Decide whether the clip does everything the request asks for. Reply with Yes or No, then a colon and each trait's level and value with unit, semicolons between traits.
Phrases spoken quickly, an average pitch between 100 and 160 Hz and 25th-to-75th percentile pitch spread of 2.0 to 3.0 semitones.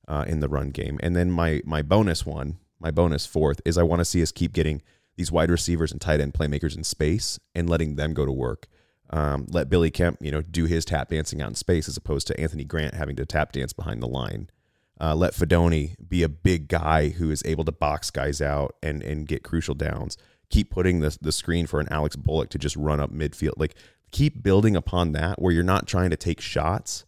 No: fast, 235 wpm; very low, 80 Hz; narrow, 2.4 semitones